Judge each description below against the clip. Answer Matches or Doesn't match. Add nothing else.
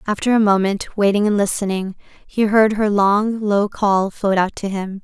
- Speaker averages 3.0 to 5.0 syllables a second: Matches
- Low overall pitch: Doesn't match